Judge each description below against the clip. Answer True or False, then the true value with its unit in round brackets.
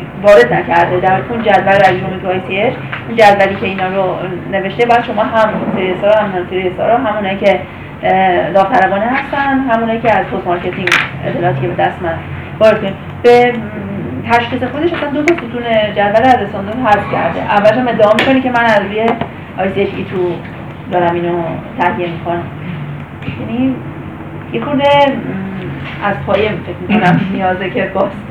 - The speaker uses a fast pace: True (165 wpm)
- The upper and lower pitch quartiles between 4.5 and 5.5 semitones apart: False (4.0 semitones)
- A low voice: False (200 Hz)